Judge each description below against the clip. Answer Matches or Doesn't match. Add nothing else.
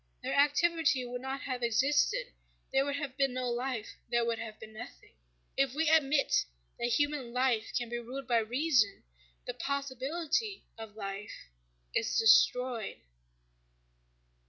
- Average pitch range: Matches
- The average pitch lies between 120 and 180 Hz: Doesn't match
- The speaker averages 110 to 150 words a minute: Matches